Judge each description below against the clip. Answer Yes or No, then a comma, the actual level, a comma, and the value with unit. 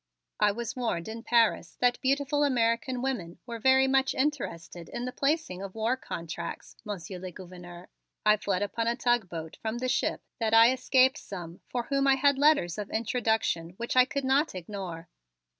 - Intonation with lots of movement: Yes, wide, 6.0 semitones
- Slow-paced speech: No, average, 180 wpm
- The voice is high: Yes, high, 230 Hz